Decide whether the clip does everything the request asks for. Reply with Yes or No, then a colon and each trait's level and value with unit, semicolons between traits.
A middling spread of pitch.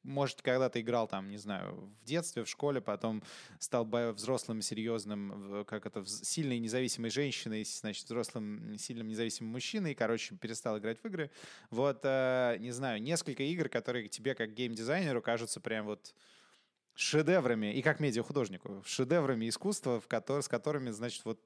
Yes: average, 3.7 semitones